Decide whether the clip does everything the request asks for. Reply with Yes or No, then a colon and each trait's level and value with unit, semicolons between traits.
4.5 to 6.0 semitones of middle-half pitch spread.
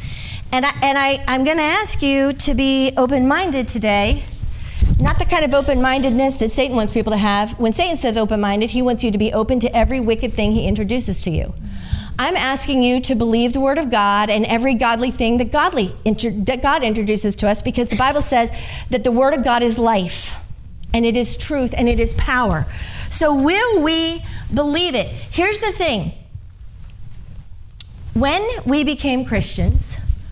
No: average, 4.1 semitones